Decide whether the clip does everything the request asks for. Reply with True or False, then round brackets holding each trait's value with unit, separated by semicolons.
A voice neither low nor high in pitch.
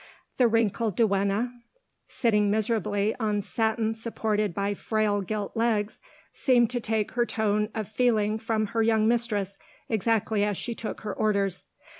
False (215 Hz)